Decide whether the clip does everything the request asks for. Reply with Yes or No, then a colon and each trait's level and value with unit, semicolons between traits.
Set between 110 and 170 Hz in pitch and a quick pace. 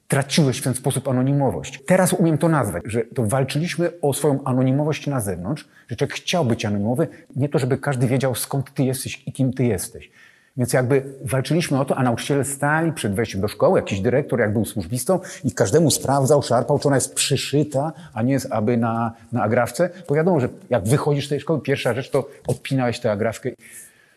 Yes: low, 135 Hz; fast, 200 wpm